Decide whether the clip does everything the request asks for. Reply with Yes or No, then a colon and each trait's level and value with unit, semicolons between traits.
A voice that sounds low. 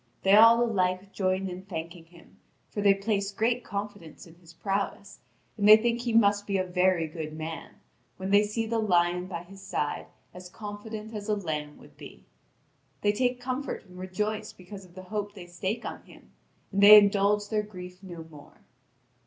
No: high, 195 Hz